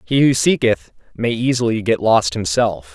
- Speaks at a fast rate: No, average, 165 wpm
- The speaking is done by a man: Yes, male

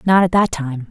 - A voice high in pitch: No, medium, 165 Hz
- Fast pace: Yes, fast, 265 wpm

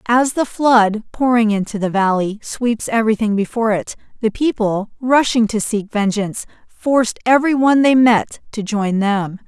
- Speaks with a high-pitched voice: Yes, high, 225 Hz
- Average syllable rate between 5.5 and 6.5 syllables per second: No, 4.8 syllables/s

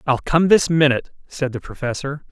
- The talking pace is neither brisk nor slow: Yes, average, 180 wpm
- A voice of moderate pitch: Yes, medium, 145 Hz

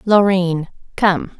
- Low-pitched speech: No, medium, 185 Hz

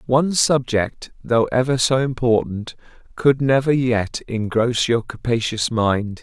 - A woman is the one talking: No, male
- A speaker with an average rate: No, slow, 125 wpm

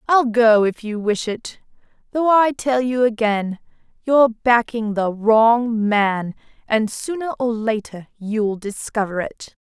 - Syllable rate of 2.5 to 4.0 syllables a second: Yes, 3.7 syllables/s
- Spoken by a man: No, female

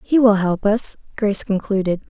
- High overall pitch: Yes, high, 205 Hz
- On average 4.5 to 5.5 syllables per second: Yes, 5.1 syllables/s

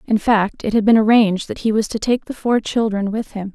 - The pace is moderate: No, fast, 270 wpm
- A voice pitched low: No, high, 215 Hz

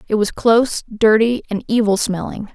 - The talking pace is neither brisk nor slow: Yes, average, 165 wpm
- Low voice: No, high, 215 Hz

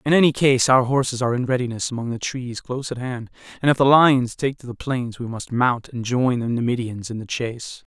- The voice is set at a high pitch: No, low, 125 Hz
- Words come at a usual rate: No, fast, 240 wpm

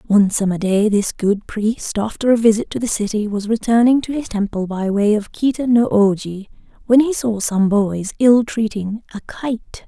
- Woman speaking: Yes, female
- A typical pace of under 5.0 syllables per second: Yes, 4.7 syllables/s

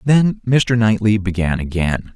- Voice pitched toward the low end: Yes, low, 105 Hz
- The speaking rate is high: No, average, 140 wpm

